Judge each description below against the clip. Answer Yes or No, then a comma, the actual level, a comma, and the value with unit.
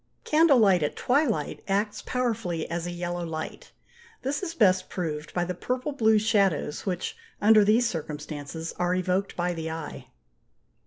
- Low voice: No, medium, 185 Hz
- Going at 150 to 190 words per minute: Yes, average, 155 wpm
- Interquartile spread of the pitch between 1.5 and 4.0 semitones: No, average, 5.0 semitones